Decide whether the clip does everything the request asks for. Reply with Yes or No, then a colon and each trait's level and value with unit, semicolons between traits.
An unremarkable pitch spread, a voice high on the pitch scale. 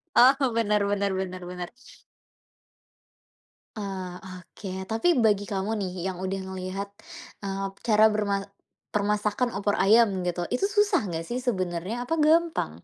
Yes: average, 3.6 semitones; high, 200 Hz